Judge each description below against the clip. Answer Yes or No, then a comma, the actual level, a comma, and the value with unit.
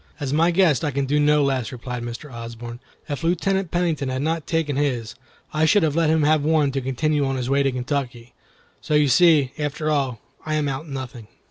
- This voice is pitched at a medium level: Yes, medium, 145 Hz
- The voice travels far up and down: No, average, 3.1 semitones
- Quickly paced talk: Yes, fast, 215 wpm